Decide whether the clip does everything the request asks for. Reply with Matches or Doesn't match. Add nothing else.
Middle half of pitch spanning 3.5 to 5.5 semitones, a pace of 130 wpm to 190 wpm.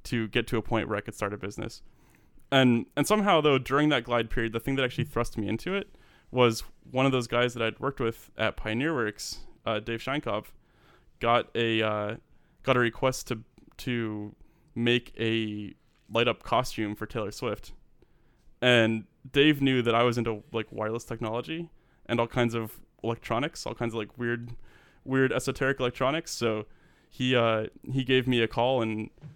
Doesn't match